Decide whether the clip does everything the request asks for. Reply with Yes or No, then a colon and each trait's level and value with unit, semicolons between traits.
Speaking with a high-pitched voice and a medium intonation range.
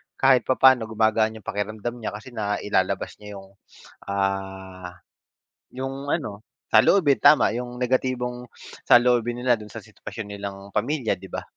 No: low, 110 Hz; average, 3.6 semitones